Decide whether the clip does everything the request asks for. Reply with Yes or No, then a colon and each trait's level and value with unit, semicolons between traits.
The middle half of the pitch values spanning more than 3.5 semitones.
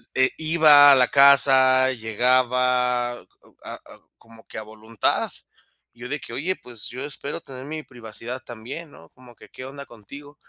No: average, 2.8 semitones